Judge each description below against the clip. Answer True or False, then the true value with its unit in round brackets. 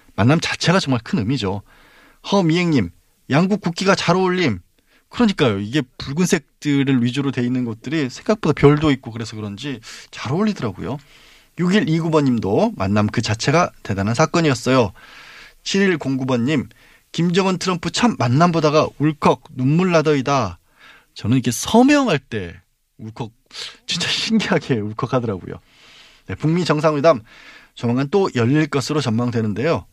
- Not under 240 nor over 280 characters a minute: False (310 characters per minute)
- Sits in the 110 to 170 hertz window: True (140 Hz)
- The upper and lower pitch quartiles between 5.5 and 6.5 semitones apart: True (6.1 semitones)